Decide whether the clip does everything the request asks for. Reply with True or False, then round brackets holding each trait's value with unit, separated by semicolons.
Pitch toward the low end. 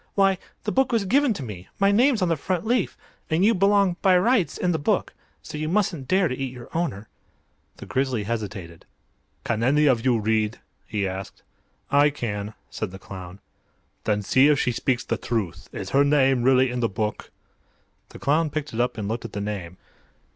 True (130 Hz)